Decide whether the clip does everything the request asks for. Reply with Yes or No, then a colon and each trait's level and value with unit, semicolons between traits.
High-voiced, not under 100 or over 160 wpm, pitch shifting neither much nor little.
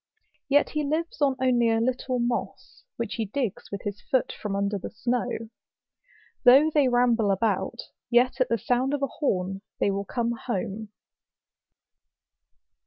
Yes: high, 240 Hz; average, 155 wpm; average, 4.0 semitones